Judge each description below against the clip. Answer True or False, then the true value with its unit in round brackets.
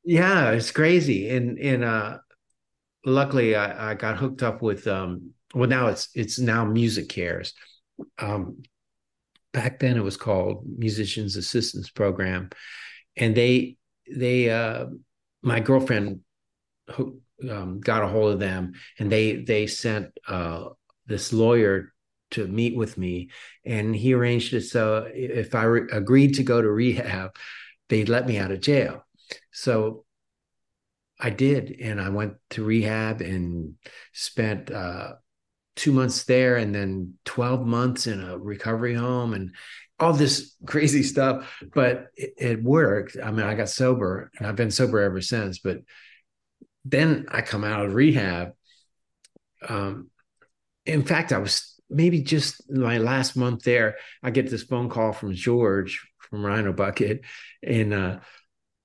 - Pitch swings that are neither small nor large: True (3.8 semitones)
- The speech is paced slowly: False (150 wpm)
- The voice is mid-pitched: False (115 Hz)